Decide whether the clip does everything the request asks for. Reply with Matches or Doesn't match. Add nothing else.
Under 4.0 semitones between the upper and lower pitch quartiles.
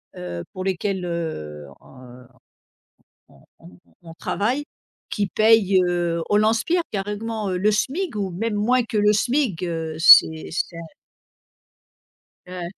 Doesn't match